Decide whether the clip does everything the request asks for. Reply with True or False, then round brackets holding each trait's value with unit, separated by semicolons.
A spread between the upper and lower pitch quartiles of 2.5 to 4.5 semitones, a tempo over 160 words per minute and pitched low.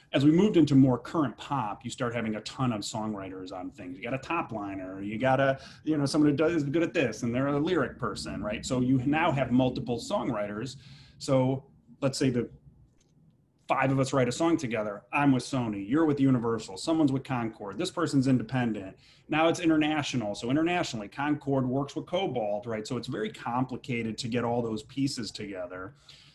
True (3.8 semitones; 200 wpm; 130 Hz)